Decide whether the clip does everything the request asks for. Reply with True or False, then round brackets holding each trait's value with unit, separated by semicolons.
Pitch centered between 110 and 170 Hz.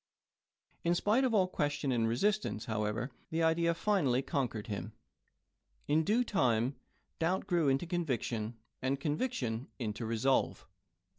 True (140 Hz)